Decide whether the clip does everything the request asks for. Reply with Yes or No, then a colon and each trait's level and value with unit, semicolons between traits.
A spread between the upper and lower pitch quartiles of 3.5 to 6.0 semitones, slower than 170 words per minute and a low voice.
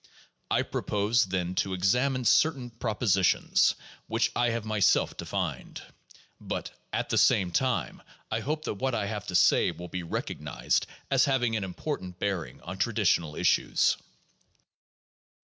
Yes: average, 4.8 semitones; average, 150 wpm; low, 105 Hz